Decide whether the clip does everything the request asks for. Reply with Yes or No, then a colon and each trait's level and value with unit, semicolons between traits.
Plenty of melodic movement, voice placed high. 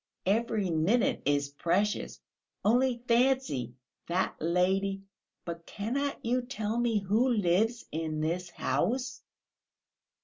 Yes: wide, 5.9 semitones; high, 205 Hz